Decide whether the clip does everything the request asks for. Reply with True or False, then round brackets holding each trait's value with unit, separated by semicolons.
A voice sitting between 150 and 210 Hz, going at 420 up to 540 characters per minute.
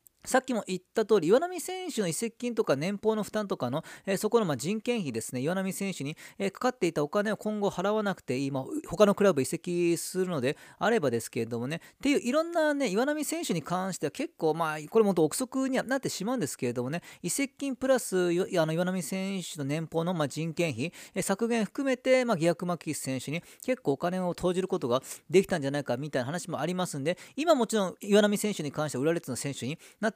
True (185 Hz; 430 characters per minute)